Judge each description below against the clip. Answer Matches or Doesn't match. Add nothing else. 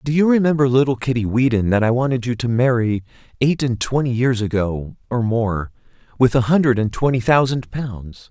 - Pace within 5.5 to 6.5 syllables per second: Doesn't match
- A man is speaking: Matches